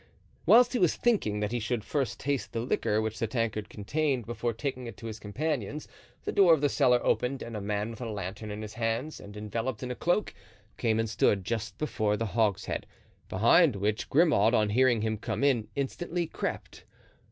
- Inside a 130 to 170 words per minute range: No, average, 200 wpm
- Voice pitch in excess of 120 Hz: No, low, 115 Hz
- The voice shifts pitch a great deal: No, average, 4.5 semitones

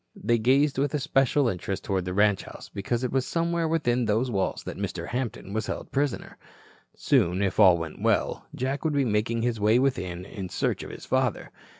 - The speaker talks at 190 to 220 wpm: Yes, average, 200 wpm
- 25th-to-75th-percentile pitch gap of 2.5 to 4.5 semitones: No, wide, 5.4 semitones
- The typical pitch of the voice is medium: No, low, 115 Hz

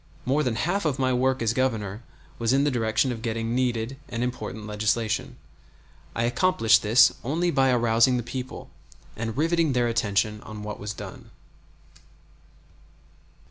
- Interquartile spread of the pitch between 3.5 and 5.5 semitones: No, average, 2.9 semitones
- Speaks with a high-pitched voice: No, low, 120 Hz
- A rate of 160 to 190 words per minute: No, average, 150 wpm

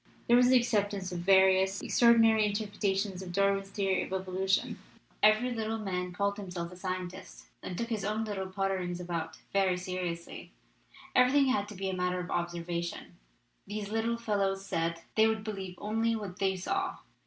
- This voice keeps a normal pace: Yes, average, 170 wpm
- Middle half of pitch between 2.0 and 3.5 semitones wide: Yes, average, 2.9 semitones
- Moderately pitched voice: No, high, 195 Hz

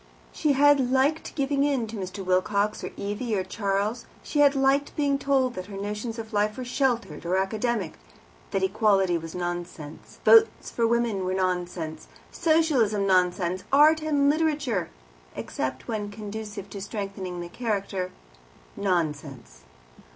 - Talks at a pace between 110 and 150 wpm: Yes, average, 140 wpm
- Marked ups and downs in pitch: Yes, wide, 6.1 semitones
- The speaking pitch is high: Yes, high, 210 Hz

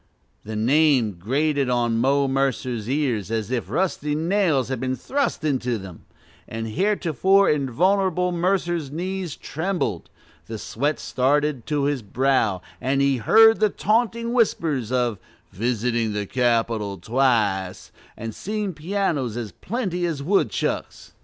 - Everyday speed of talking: No, slow, 130 wpm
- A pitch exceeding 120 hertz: Yes, low, 135 Hz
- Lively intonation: Yes, wide, 7.2 semitones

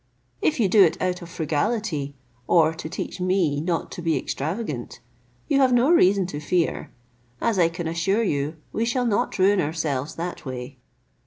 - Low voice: No, medium, 170 Hz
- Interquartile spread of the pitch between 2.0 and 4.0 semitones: No, average, 4.6 semitones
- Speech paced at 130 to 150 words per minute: No, average, 175 wpm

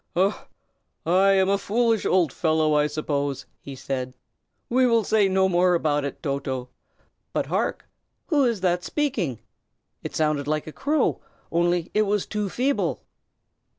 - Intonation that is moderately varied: No, wide, 5.9 semitones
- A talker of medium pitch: Yes, medium, 175 Hz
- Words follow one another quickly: No, average, 150 wpm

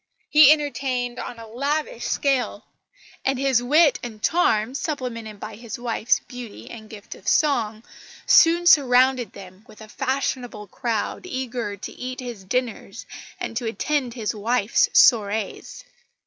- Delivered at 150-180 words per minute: No, average, 140 wpm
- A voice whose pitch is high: Yes, high, 245 Hz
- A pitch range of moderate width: Yes, average, 3.6 semitones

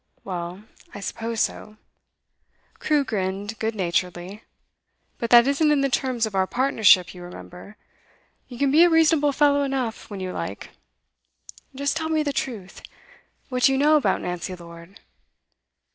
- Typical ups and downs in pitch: No, wide, 6.9 semitones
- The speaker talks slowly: No, average, 155 wpm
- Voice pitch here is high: Yes, high, 230 Hz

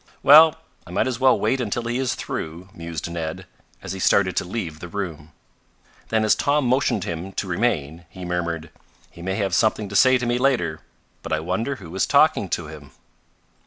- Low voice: Yes, very low, 95 Hz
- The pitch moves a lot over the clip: Yes, wide, 6.4 semitones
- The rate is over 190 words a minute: Yes, average, 200 wpm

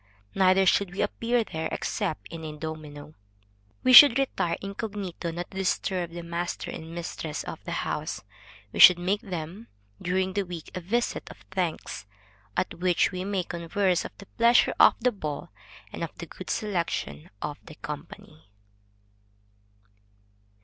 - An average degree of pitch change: Yes, average, 3.5 semitones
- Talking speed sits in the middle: Yes, average, 155 wpm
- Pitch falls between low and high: Yes, medium, 180 Hz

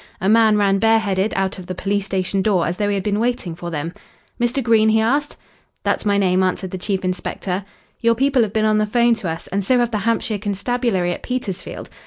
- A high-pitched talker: Yes, high, 205 Hz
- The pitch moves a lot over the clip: No, average, 3.3 semitones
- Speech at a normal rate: No, fast, 235 wpm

